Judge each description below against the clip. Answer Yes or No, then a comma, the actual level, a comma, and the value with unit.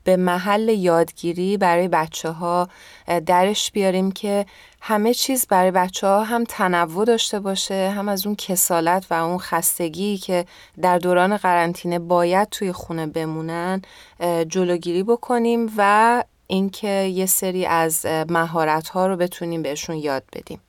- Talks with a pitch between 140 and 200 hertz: Yes, medium, 185 Hz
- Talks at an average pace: Yes, average, 135 wpm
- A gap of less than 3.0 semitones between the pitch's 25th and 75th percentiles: Yes, narrow, 2.6 semitones